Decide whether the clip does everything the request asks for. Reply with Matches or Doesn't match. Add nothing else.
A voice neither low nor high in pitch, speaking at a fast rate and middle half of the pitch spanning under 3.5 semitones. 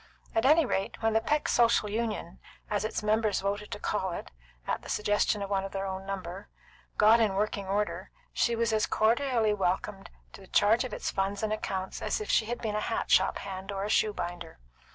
Doesn't match